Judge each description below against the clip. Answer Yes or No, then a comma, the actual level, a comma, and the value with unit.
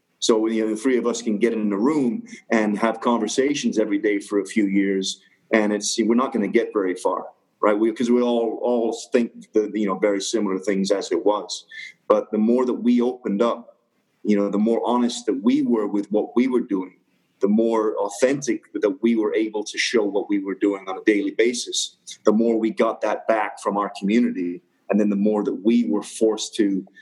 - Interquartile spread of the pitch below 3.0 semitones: Yes, narrow, 2.6 semitones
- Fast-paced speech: Yes, fast, 225 wpm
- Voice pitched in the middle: No, low, 110 Hz